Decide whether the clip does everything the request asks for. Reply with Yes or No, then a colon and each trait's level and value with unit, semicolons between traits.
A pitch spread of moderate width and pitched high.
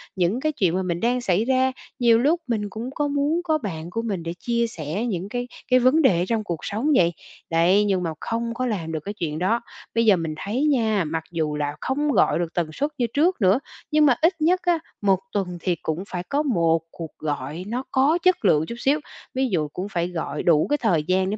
No: wide, 7.1 semitones; high, 210 Hz